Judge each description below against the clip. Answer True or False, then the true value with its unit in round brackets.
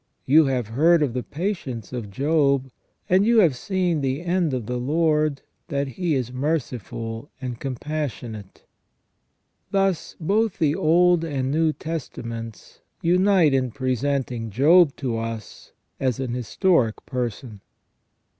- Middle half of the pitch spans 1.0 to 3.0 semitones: False (4.9 semitones)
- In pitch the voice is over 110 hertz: True (140 Hz)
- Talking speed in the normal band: False (130 wpm)